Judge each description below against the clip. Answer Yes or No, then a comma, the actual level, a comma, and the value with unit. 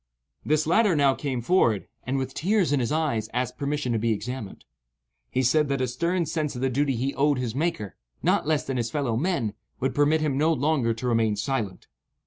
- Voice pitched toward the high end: No, low, 135 Hz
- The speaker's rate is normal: No, fast, 210 wpm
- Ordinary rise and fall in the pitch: Yes, average, 4.3 semitones